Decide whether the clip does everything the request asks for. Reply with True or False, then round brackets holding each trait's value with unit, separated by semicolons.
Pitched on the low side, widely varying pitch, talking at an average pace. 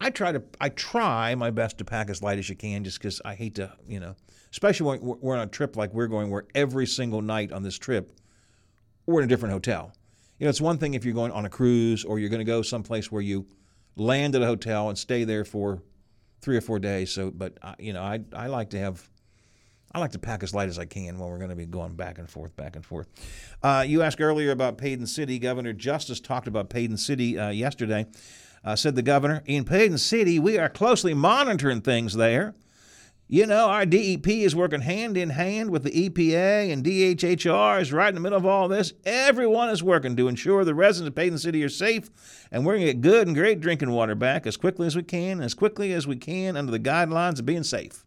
False (120 Hz; 7.9 semitones; 240 wpm)